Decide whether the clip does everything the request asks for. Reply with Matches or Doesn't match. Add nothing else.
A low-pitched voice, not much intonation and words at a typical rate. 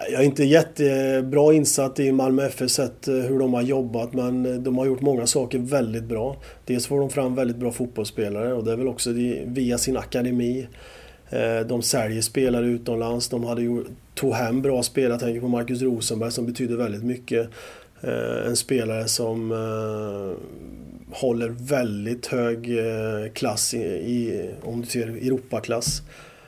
Matches